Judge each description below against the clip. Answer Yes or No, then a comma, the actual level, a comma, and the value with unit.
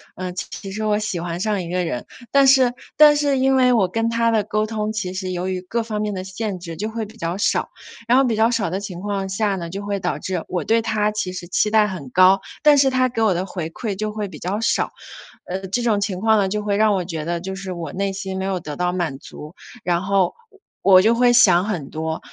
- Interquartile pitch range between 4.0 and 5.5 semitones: No, average, 3.3 semitones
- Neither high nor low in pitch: No, high, 200 Hz